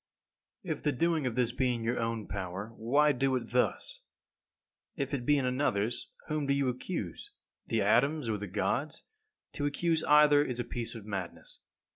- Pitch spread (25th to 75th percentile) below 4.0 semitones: No, average, 4.4 semitones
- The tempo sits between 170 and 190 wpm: Yes, average, 185 wpm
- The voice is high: No, low, 125 Hz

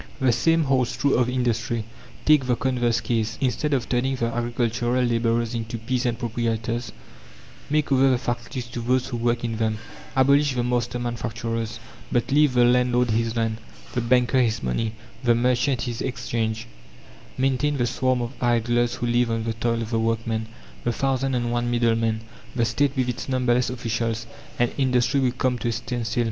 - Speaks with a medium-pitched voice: No, low, 120 Hz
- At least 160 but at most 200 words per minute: Yes, average, 180 wpm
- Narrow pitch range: Yes, narrow, 1.7 semitones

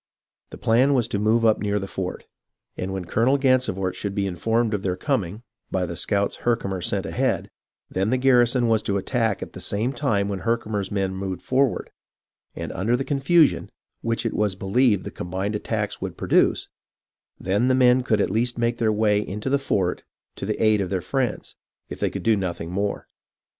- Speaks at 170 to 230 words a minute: Yes, average, 195 wpm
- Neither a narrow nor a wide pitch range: Yes, average, 3.9 semitones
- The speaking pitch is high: No, low, 105 Hz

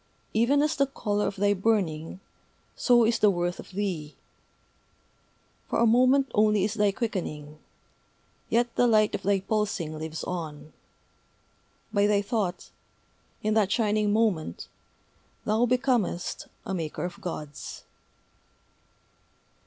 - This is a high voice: Yes, high, 205 Hz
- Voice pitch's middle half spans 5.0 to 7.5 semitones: No, average, 4.3 semitones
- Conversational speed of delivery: No, slow, 125 wpm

